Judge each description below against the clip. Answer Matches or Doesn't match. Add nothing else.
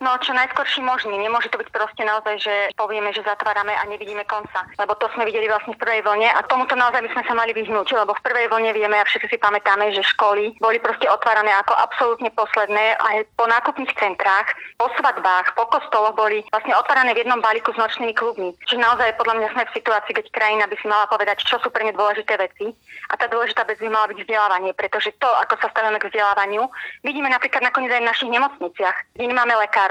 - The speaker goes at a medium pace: Doesn't match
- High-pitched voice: Matches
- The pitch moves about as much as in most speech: Doesn't match